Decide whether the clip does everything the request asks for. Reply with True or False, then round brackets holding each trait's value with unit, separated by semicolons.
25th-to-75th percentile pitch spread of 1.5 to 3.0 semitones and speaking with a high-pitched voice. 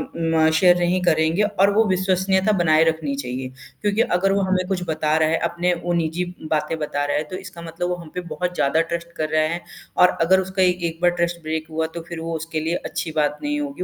False (2.4 semitones; 170 Hz)